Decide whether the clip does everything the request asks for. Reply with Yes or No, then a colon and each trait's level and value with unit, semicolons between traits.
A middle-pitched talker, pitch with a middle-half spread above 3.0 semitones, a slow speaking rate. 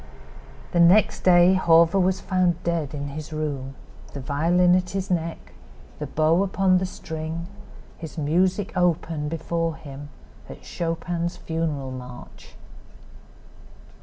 No: medium, 165 Hz; average, 2.7 semitones; slow, 125 wpm